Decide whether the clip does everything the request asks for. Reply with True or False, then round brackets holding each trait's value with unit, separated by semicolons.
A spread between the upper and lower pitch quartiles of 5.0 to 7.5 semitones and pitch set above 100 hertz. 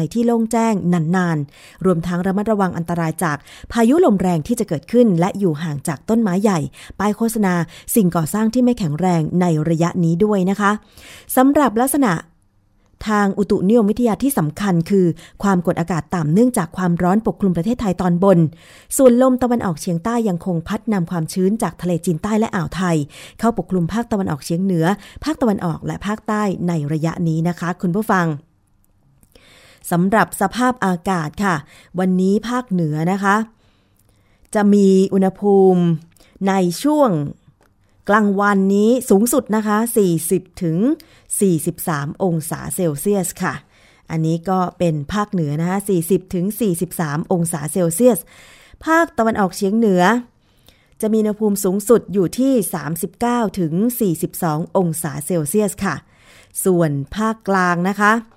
False (4.0 semitones; 185 Hz)